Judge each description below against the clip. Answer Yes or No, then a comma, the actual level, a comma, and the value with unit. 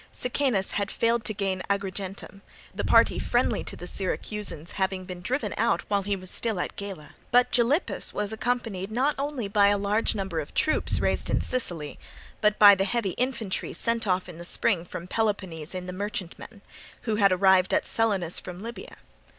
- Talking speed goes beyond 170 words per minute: Yes, average, 185 wpm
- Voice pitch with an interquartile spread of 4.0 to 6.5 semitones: No, average, 3.4 semitones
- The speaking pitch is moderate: No, high, 200 Hz